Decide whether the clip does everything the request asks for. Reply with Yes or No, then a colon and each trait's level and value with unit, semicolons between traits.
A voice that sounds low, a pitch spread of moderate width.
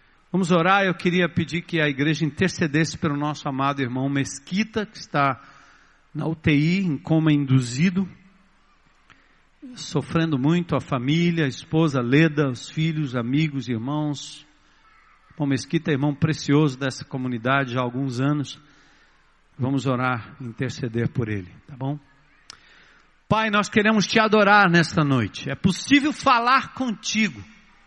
No: medium, 150 Hz; average, 4.4 semitones